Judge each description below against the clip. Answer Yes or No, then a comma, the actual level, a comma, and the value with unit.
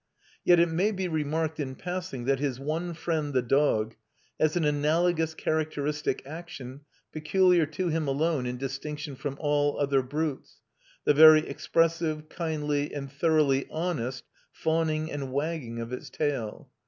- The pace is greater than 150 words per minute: No, average, 145 wpm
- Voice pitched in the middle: Yes, medium, 150 Hz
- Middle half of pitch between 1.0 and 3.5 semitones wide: Yes, average, 2.8 semitones